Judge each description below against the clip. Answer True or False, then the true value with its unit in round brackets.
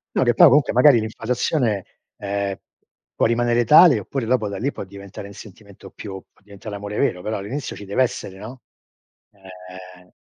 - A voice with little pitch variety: False (3.6 semitones)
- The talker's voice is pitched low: True (105 Hz)